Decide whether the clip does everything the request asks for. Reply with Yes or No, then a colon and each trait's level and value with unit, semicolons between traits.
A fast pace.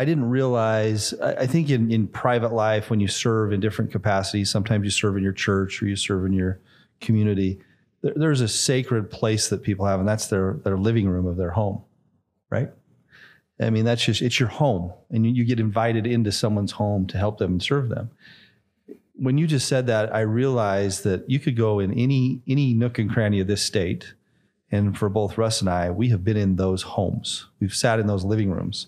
Yes: fast, 215 wpm